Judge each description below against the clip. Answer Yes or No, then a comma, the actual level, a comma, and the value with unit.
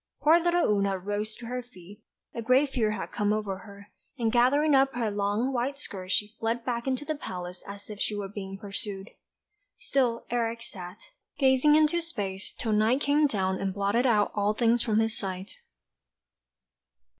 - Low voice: No, high, 220 Hz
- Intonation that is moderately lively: Yes, average, 4.1 semitones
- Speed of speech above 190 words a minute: No, average, 180 wpm